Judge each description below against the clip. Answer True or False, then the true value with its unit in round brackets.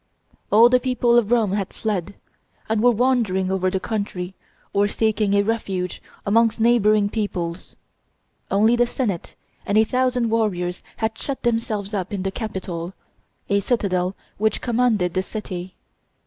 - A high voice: True (210 Hz)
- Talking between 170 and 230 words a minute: False (150 wpm)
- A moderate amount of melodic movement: True (3.3 semitones)